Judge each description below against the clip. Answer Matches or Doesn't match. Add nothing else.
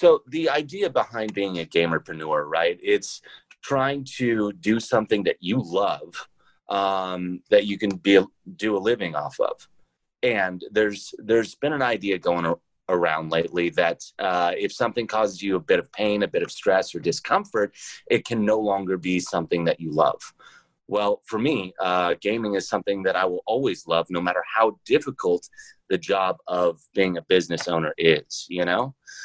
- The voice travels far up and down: Doesn't match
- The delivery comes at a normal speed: Matches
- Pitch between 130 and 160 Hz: Doesn't match